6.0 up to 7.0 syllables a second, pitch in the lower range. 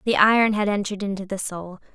No: 6.4 syllables/s; high, 200 Hz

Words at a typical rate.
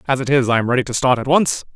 No: fast, 340 wpm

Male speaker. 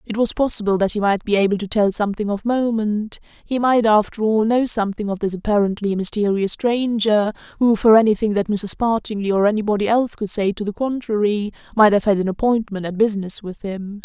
No: female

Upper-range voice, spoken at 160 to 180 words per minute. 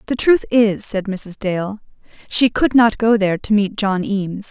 No: high, 210 Hz; average, 200 wpm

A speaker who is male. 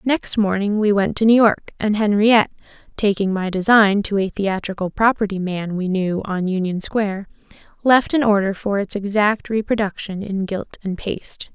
No: female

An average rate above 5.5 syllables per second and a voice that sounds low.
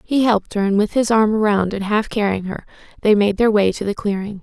No: 5.8 syllables/s; high, 210 Hz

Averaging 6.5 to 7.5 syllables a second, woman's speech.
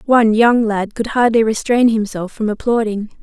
No: 5.0 syllables/s; female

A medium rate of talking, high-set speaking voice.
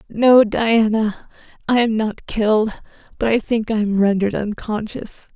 Yes: average, 145 wpm; high, 215 Hz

